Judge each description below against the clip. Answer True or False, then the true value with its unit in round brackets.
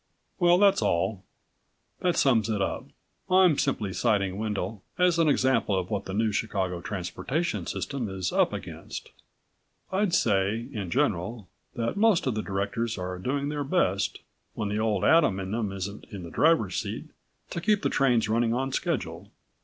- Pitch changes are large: True (6.7 semitones)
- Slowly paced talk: False (170 wpm)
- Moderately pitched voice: False (110 Hz)